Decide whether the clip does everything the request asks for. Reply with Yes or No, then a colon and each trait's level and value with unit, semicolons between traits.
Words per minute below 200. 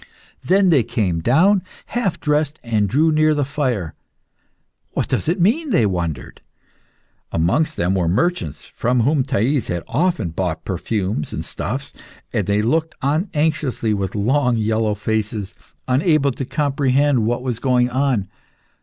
Yes: average, 145 wpm